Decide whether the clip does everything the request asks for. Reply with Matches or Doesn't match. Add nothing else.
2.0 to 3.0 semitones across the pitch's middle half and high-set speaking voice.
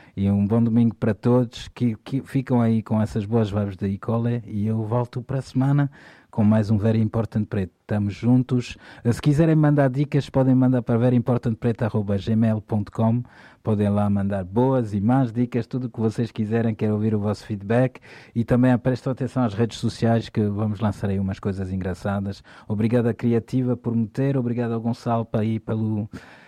Doesn't match